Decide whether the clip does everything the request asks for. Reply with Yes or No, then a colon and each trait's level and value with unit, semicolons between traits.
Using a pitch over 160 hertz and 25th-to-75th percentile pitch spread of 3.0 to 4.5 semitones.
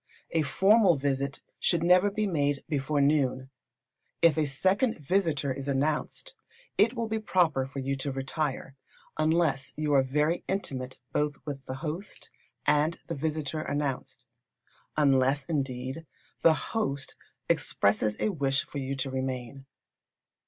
No: medium, 145 Hz; average, 3.5 semitones